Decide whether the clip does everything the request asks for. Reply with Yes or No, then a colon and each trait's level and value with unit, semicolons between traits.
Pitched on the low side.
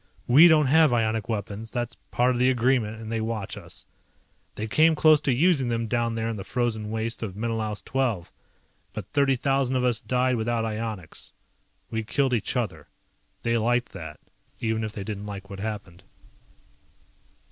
Yes: low, 115 Hz